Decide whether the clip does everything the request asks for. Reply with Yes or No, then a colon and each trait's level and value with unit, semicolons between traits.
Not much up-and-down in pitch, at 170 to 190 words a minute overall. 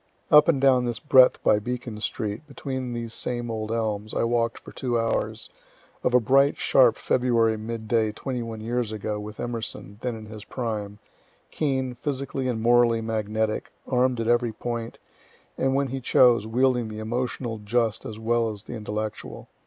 Yes: narrow, 2.3 semitones; average, 175 wpm